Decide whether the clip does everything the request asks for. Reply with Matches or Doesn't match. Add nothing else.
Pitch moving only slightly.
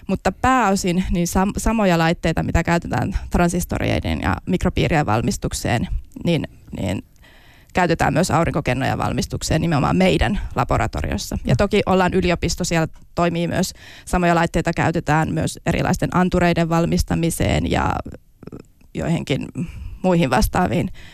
Doesn't match